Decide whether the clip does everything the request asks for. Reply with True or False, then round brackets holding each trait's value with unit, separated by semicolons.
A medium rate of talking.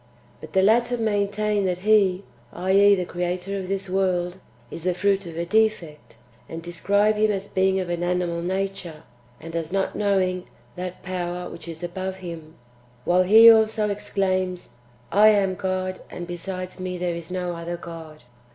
True (170 wpm)